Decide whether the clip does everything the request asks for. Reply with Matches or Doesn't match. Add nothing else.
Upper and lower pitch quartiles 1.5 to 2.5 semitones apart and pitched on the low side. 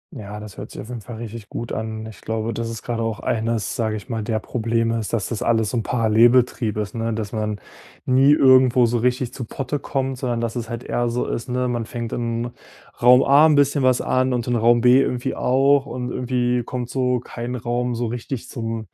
Matches